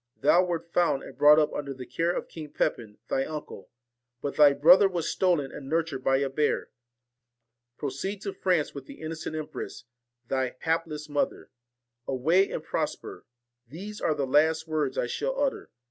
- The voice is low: No, medium, 155 Hz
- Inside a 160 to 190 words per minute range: Yes, average, 170 wpm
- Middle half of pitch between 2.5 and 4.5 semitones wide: Yes, average, 3.5 semitones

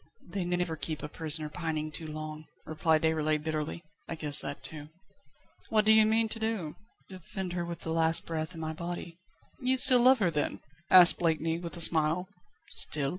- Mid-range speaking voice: Yes, medium, 165 Hz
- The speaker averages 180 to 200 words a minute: Yes, average, 185 wpm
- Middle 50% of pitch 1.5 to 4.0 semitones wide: Yes, narrow, 2.5 semitones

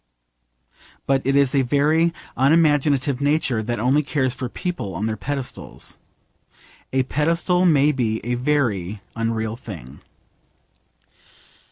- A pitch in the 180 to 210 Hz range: No, low, 135 Hz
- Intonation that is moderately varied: Yes, average, 4.3 semitones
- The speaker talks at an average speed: No, slow, 120 wpm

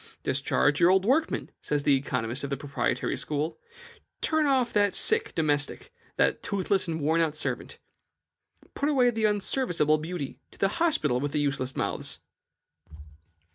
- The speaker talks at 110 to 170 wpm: Yes, average, 150 wpm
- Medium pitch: Yes, medium, 165 Hz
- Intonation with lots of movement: Yes, wide, 7.2 semitones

